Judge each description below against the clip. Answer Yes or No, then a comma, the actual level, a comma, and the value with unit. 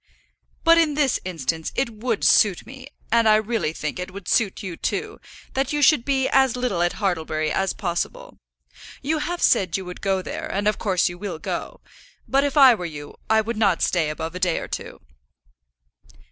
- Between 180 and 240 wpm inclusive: Yes, average, 200 wpm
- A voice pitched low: No, high, 205 Hz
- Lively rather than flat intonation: Yes, wide, 6.9 semitones